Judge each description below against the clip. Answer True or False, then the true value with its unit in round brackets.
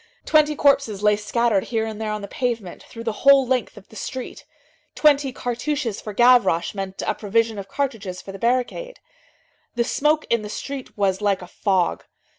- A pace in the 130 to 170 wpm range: False (185 wpm)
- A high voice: True (230 Hz)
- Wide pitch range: False (4.3 semitones)